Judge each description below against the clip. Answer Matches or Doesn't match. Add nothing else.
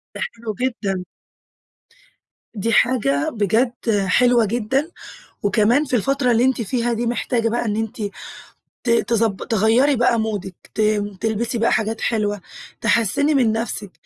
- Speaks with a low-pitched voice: Doesn't match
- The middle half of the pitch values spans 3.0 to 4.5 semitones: Doesn't match